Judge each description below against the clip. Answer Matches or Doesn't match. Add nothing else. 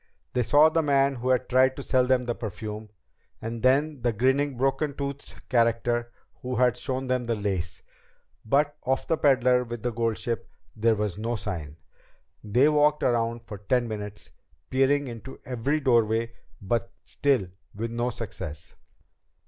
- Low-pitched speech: Matches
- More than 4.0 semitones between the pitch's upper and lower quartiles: Doesn't match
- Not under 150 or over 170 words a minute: Matches